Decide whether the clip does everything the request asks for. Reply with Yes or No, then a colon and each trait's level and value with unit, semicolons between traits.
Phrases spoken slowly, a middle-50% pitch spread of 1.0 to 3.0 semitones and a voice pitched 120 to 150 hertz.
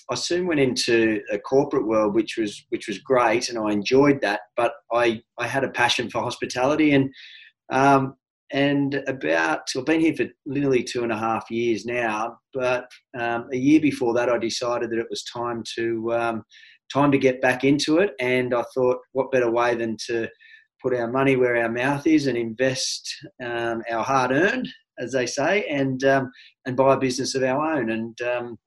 No: average, 200 wpm; average, 2.7 semitones; low, 125 Hz